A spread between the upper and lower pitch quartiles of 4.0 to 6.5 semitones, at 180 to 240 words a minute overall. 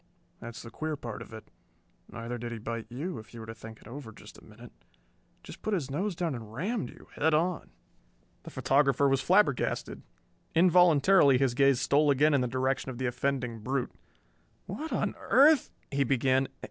Yes: average, 4.8 semitones; average, 185 wpm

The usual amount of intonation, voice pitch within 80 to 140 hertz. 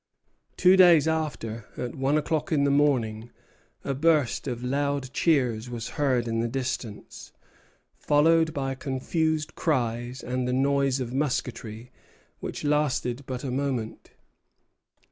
Yes: average, 3.2 semitones; low, 135 Hz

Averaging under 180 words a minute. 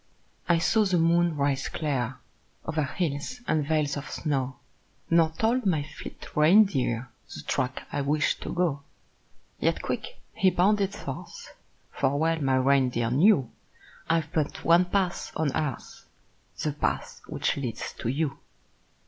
Yes: average, 140 wpm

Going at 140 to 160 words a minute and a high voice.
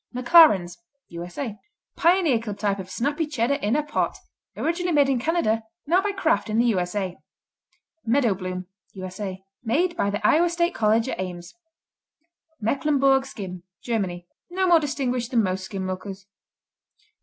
Yes: average, 145 wpm; high, 230 Hz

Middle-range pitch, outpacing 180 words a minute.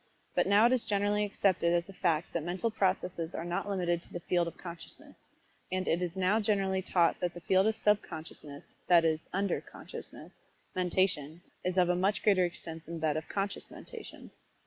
Yes: medium, 180 Hz; average, 195 wpm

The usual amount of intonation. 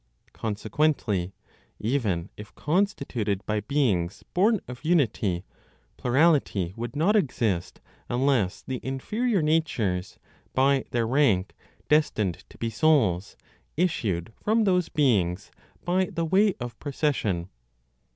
No: wide, 7.6 semitones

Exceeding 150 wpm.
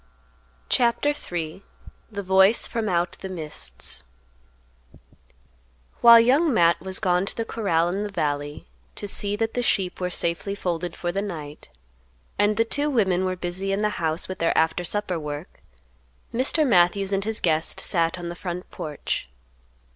Yes: average, 160 wpm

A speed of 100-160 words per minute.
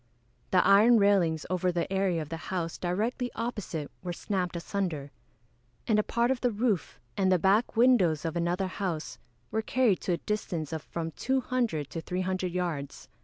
No: average, 170 wpm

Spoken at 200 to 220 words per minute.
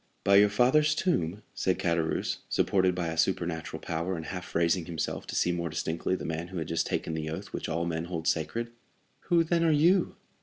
Yes: fast, 205 wpm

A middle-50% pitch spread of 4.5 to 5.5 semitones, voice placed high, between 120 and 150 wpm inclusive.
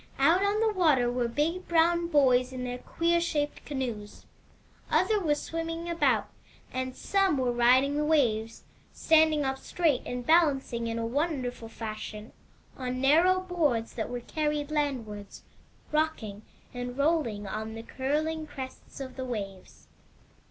Yes: average, 4.9 semitones; very high, 275 Hz; average, 145 wpm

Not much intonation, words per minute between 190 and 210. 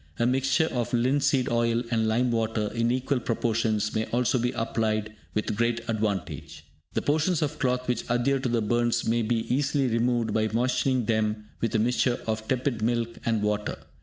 No: narrow, 2.3 semitones; average, 180 wpm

